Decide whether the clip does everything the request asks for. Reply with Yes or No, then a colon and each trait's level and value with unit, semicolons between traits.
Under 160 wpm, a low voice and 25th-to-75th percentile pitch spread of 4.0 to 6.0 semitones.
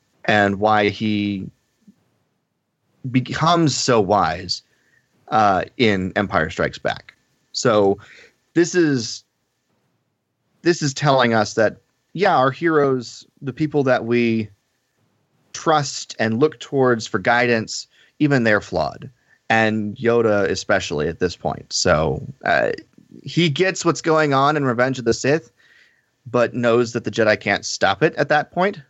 Yes: slow, 135 wpm; low, 125 Hz; average, 5.0 semitones